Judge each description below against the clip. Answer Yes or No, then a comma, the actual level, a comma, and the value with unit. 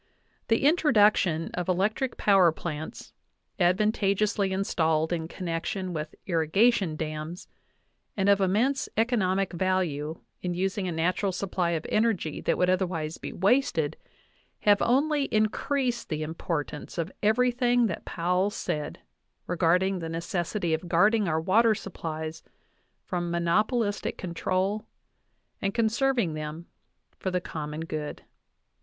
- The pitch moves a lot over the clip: No, average, 4.4 semitones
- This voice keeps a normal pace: No, slow, 125 wpm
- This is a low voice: No, medium, 185 Hz